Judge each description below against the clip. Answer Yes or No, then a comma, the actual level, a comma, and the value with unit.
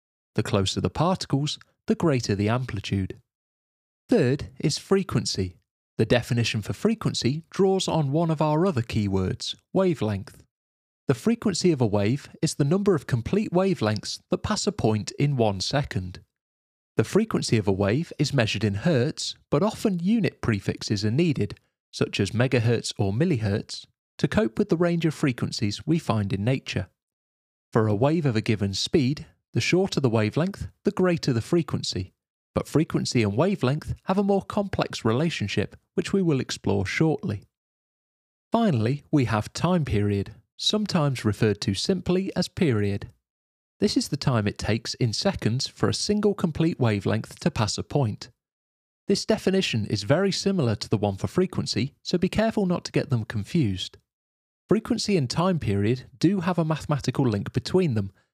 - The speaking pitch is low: Yes, low, 125 Hz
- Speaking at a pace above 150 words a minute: Yes, average, 165 wpm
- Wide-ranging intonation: Yes, wide, 8.7 semitones